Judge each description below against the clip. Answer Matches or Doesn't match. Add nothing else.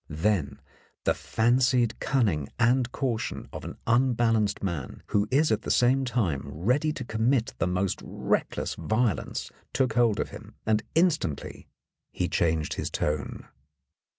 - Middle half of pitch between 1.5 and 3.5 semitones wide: Doesn't match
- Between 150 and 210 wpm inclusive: Doesn't match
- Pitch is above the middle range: Doesn't match